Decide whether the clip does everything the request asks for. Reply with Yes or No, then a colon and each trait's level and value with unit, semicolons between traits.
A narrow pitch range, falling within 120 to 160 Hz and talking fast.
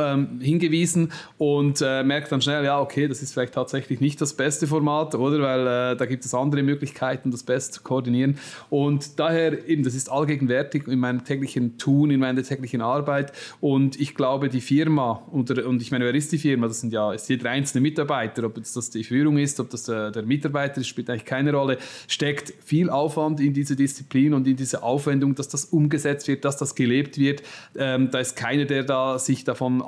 Yes: narrow, 2.1 semitones; medium, 140 Hz; fast, 205 wpm